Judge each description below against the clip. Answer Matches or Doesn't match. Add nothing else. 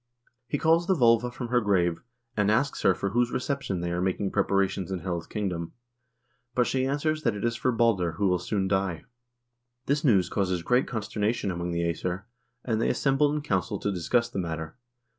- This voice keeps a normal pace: Matches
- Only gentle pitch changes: Doesn't match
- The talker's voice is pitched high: Doesn't match